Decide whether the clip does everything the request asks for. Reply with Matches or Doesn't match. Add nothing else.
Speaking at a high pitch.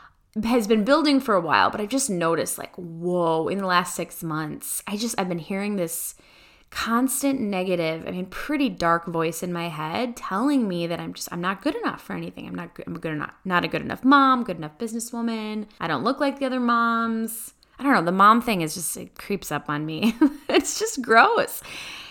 Matches